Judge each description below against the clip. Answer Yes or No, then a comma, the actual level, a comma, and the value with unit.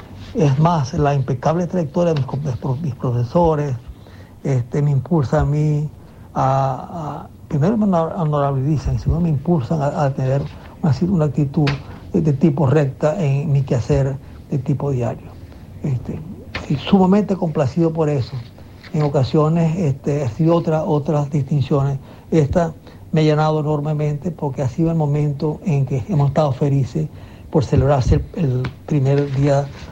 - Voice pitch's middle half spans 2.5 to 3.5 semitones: Yes, average, 2.8 semitones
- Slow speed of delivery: No, average, 145 wpm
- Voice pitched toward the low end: No, medium, 145 Hz